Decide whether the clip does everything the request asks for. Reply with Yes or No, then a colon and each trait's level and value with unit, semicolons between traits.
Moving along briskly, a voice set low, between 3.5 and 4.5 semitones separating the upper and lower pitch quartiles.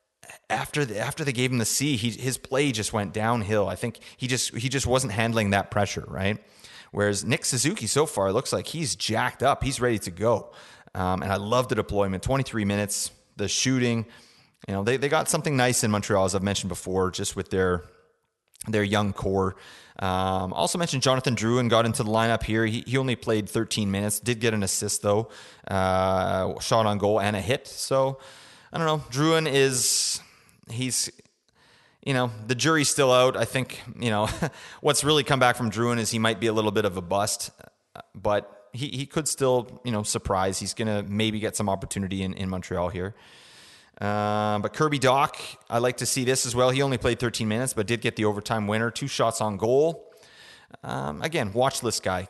Yes: fast, 210 wpm; low, 115 Hz; average, 3.9 semitones